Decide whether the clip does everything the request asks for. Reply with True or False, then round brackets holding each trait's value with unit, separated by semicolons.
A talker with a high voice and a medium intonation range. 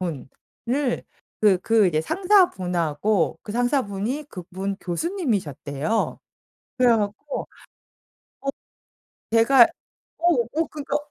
False (220 Hz; 7.1 semitones)